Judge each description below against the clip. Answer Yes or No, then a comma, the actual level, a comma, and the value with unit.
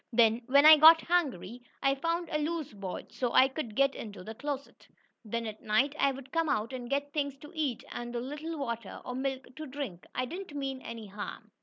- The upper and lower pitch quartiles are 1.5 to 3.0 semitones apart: No, average, 4.1 semitones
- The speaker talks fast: Yes, fast, 215 wpm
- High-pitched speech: Yes, very high, 270 Hz